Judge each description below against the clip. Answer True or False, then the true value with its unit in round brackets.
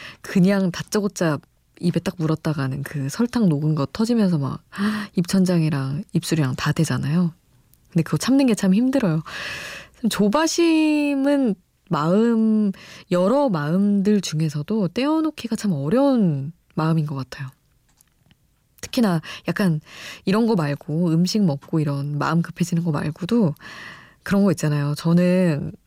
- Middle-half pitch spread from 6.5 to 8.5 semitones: False (5.6 semitones)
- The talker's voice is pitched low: False (175 Hz)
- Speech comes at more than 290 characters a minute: False (270 characters per minute)